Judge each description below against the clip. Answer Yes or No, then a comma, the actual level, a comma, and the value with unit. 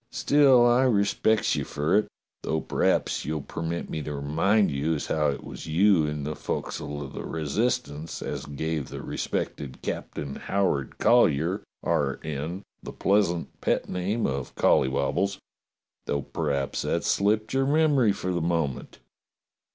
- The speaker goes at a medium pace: Yes, average, 150 wpm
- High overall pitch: No, very low, 80 Hz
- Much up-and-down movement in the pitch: Yes, wide, 6.1 semitones